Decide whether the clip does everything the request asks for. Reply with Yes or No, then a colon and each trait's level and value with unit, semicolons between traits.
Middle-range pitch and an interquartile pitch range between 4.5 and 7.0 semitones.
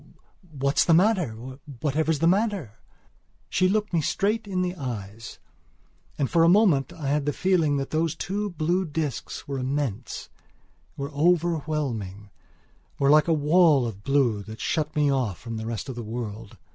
Yes: medium, 145 Hz; wide, 5.6 semitones